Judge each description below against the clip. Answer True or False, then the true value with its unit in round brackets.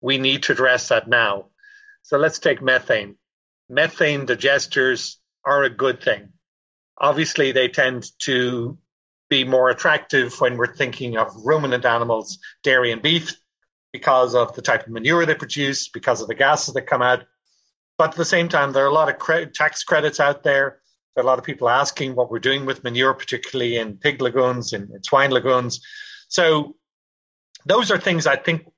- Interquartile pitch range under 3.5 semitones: False (3.8 semitones)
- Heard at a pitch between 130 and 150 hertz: True (135 Hz)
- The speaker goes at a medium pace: True (180 wpm)